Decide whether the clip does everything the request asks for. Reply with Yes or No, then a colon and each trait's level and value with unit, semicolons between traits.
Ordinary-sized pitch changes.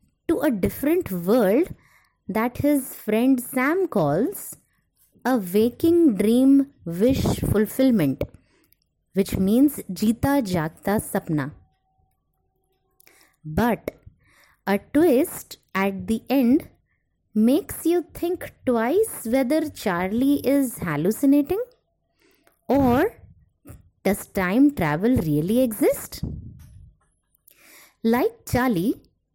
No: wide, 6.5 semitones